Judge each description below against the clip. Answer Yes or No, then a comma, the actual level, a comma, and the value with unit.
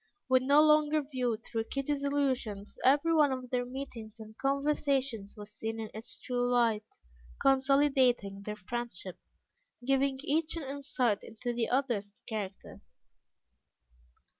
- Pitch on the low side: No, very high, 255 Hz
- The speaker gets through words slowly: Yes, slow, 130 wpm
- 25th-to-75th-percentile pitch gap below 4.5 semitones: Yes, average, 4.1 semitones